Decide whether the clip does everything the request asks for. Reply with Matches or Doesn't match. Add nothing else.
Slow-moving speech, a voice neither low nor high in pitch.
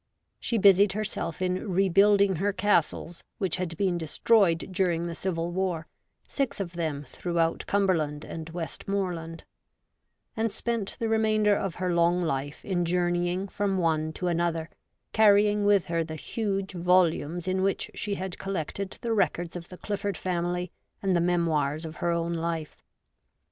Doesn't match